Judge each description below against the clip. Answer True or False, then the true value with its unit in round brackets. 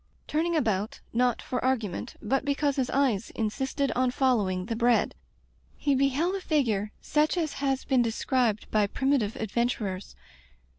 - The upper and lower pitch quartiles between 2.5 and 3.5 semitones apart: False (4.1 semitones)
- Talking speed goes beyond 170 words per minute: False (145 wpm)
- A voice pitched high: True (250 Hz)